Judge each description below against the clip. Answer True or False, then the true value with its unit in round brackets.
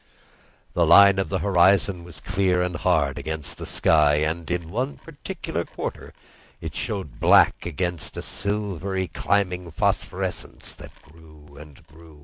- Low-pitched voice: True (85 Hz)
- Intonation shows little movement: False (3.6 semitones)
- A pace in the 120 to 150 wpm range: True (140 wpm)